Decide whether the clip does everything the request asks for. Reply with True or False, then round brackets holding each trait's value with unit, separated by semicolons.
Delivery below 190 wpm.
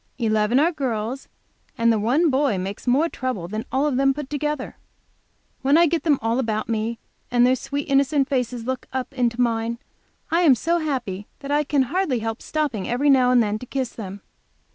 False (205 wpm)